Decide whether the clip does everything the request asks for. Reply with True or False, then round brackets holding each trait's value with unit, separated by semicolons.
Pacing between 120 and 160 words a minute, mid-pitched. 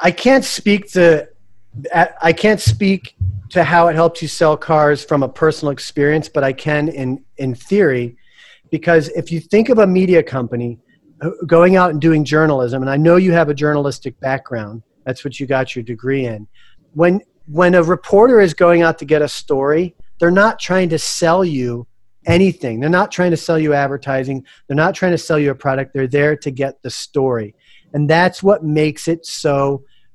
False (195 wpm; 150 Hz)